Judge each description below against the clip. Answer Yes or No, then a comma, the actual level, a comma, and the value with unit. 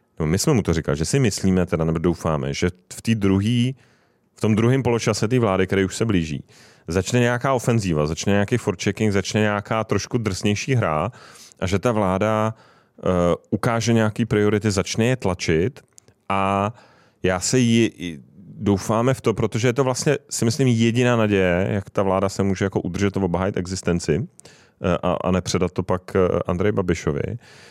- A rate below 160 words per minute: No, fast, 170 wpm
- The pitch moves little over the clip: No, average, 4.0 semitones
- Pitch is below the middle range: Yes, low, 100 Hz